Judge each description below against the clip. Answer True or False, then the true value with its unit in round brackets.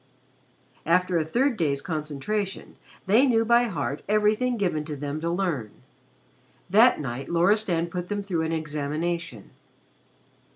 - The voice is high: False (170 Hz)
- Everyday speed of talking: False (130 wpm)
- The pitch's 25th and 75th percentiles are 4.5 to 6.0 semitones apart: True (5.6 semitones)